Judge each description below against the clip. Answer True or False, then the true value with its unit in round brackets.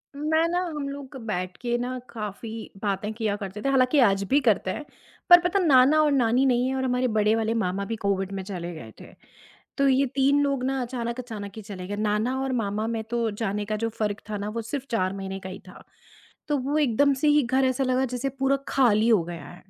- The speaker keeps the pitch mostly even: False (4.6 semitones)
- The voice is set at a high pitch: True (235 Hz)